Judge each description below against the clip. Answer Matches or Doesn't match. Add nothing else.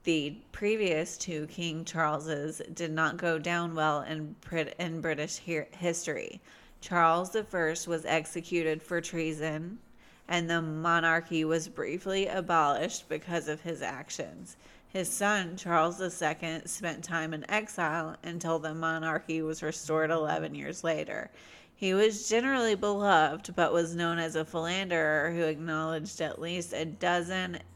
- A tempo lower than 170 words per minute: Matches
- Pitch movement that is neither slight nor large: Doesn't match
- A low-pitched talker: Doesn't match